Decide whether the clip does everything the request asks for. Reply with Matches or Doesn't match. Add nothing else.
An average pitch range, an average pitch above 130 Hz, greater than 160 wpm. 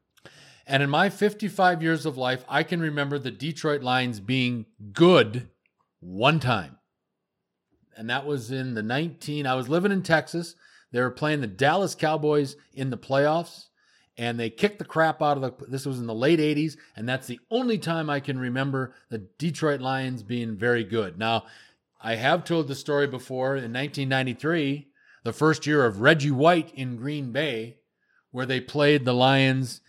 Matches